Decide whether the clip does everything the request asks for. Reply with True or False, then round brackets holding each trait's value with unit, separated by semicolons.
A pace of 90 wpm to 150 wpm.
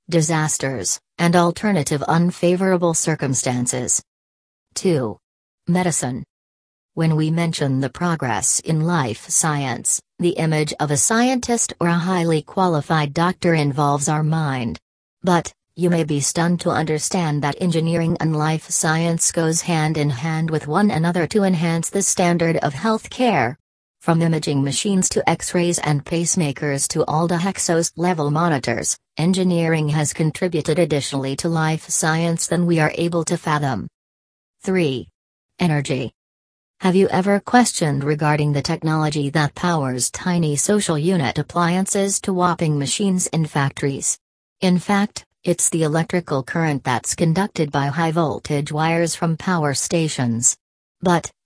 True (135 wpm)